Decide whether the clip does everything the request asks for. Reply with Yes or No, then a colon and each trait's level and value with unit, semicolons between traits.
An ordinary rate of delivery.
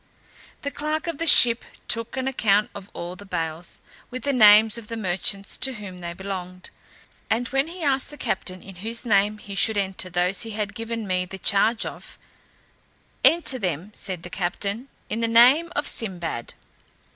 Yes: average, 180 wpm